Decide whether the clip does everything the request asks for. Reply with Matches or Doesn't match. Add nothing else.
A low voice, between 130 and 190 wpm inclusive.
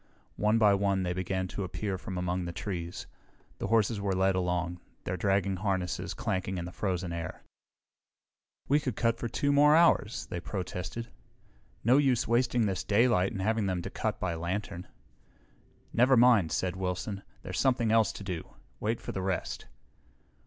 Matches